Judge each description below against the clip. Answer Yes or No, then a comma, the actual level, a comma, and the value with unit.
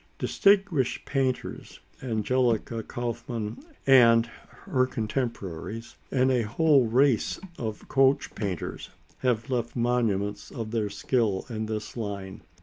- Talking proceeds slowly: Yes, slow, 110 wpm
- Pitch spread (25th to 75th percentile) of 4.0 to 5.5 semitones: No, average, 3.2 semitones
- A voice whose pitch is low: Yes, low, 115 Hz